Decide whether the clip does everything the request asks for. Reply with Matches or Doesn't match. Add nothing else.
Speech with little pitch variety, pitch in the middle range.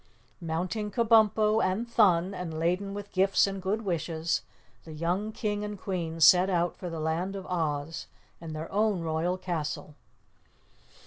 Doesn't match